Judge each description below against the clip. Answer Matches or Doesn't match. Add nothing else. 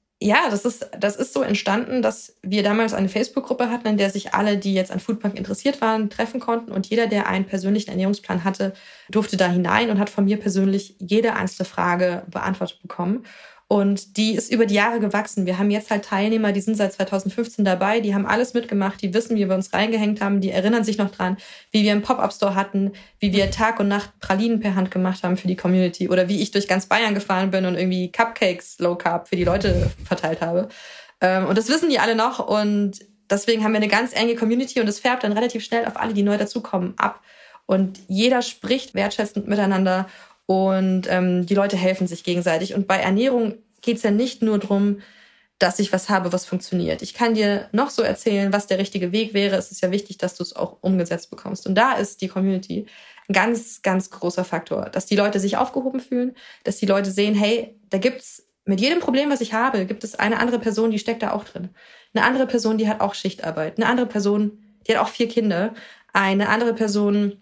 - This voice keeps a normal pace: Doesn't match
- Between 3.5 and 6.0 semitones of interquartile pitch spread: Doesn't match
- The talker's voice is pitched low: Doesn't match